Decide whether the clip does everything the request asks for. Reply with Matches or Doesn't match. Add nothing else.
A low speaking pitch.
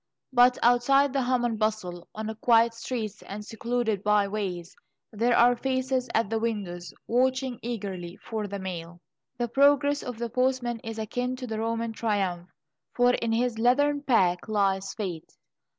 Doesn't match